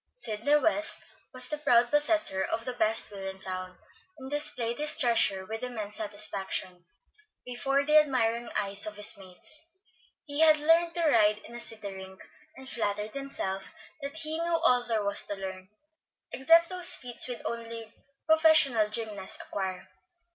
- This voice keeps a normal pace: Yes, average, 160 wpm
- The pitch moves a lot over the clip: Yes, wide, 6.3 semitones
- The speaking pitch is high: Yes, high, 235 Hz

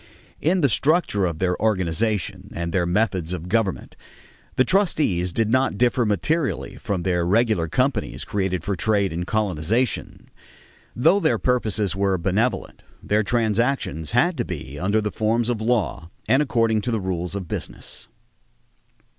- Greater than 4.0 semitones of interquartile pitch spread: Yes, average, 4.7 semitones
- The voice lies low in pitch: Yes, low, 105 Hz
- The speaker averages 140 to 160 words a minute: Yes, average, 150 wpm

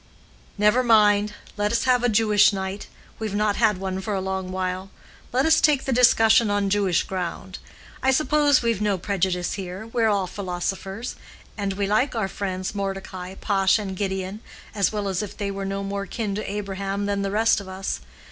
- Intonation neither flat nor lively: No, narrow, 2.1 semitones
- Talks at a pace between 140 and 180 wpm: No, average, 190 wpm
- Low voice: No, high, 200 Hz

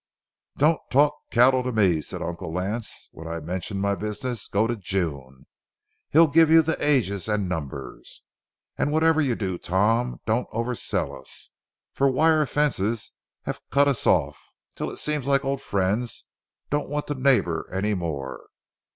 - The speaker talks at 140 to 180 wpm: Yes, average, 155 wpm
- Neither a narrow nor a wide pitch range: No, wide, 7.0 semitones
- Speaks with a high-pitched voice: No, low, 115 Hz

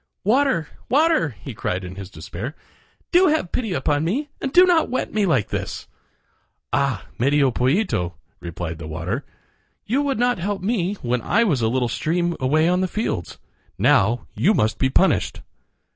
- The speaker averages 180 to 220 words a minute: No, average, 170 wpm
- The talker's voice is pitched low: No, medium, 155 Hz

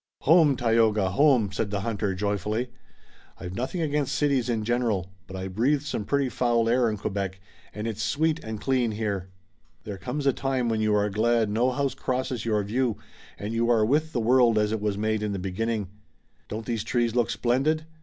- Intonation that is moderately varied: Yes, average, 3.5 semitones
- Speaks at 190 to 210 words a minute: Yes, average, 195 wpm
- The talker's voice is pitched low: Yes, low, 115 Hz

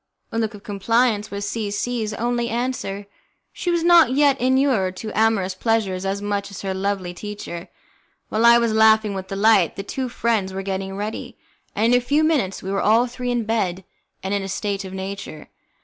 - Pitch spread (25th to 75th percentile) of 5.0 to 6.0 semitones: No, average, 3.4 semitones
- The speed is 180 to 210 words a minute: Yes, average, 200 wpm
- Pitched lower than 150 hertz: No, high, 210 Hz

